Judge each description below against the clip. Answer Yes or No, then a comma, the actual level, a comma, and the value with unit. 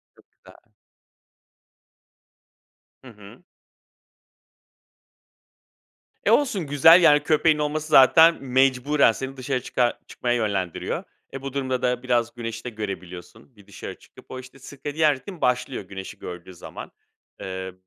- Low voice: Yes, low, 130 Hz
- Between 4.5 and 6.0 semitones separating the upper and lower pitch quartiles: Yes, average, 4.9 semitones